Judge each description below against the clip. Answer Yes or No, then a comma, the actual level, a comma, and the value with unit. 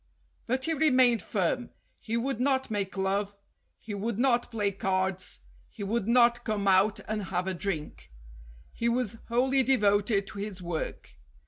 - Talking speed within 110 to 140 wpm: No, average, 155 wpm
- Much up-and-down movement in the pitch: No, average, 3.7 semitones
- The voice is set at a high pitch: Yes, high, 215 Hz